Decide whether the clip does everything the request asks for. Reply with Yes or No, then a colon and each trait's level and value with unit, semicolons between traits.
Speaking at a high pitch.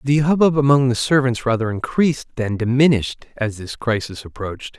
No: low, 125 Hz